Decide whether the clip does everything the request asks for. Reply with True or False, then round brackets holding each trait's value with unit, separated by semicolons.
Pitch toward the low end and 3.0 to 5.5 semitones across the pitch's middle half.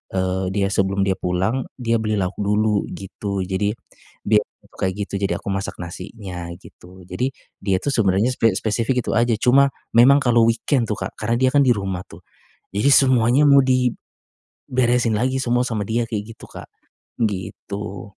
True (105 Hz; 3.7 semitones)